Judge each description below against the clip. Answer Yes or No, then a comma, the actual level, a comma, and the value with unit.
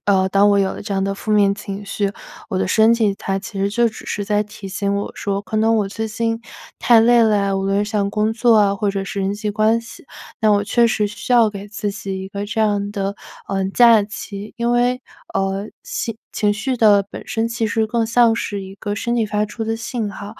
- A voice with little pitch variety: Yes, narrow, 2.0 semitones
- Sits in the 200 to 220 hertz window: Yes, high, 210 Hz